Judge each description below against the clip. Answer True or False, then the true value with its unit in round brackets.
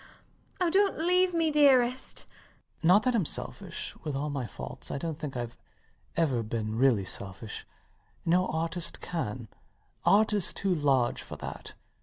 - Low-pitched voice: False (165 Hz)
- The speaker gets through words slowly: False (155 wpm)